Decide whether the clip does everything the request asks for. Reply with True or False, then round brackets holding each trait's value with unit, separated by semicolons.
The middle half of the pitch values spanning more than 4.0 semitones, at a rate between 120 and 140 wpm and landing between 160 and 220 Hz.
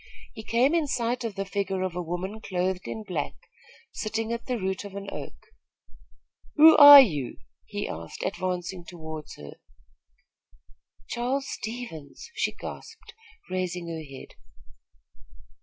True (5.0 semitones; 135 wpm; 190 Hz)